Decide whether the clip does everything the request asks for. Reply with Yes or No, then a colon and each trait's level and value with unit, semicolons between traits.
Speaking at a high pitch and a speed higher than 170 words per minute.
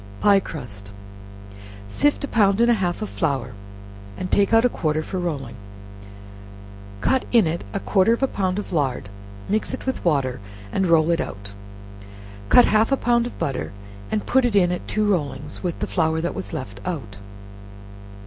No: medium, 180 Hz; average, 180 wpm